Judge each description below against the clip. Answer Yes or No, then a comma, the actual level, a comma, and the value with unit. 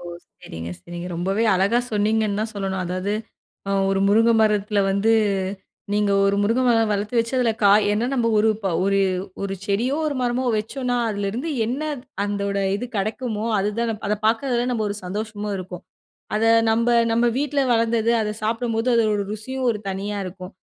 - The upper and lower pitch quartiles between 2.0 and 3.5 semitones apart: Yes, average, 2.7 semitones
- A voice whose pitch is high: Yes, high, 215 Hz